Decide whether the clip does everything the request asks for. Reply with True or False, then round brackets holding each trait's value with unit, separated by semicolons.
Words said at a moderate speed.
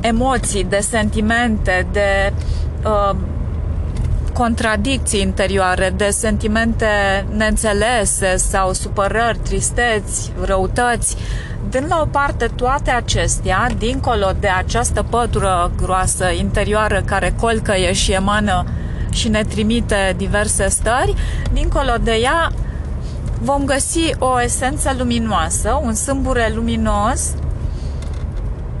False (95 wpm)